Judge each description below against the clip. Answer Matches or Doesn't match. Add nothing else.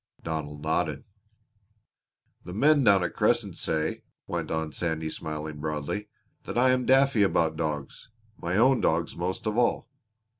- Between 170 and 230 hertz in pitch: Doesn't match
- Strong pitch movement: Matches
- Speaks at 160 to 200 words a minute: Doesn't match